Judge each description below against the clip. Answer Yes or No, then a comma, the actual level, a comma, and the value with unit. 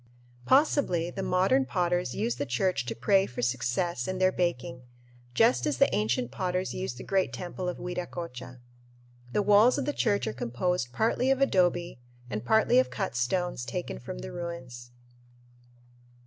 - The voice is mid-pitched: Yes, medium, 175 Hz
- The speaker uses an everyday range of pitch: No, wide, 7.5 semitones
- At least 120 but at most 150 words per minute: No, average, 160 wpm